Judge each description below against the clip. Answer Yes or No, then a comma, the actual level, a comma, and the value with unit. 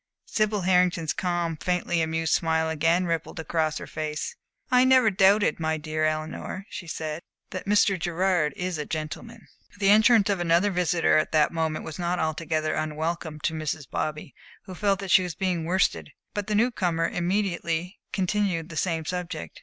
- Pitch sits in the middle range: Yes, medium, 170 Hz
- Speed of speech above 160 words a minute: Yes, average, 170 wpm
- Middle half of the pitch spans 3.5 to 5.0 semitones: No, average, 3.1 semitones